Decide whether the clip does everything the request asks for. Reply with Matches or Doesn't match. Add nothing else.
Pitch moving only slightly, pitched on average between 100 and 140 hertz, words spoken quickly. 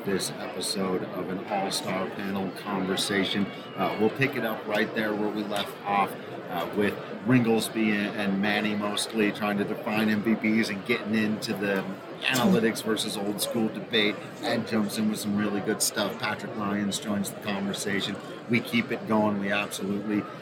Doesn't match